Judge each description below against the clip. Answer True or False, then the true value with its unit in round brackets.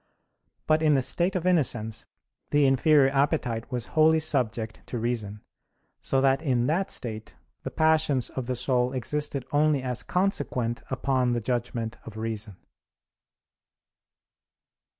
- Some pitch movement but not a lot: True (4.1 semitones)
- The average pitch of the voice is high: False (130 Hz)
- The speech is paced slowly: True (130 wpm)